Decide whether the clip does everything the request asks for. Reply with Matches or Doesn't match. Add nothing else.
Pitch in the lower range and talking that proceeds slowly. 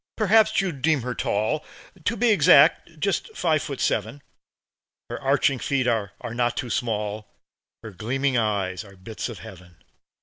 Doesn't match